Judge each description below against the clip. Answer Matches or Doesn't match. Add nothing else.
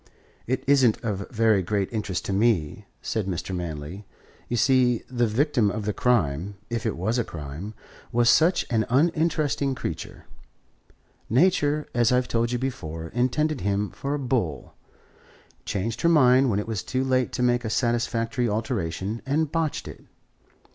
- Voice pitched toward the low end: Matches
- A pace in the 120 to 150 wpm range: Doesn't match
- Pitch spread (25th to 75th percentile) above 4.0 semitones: Matches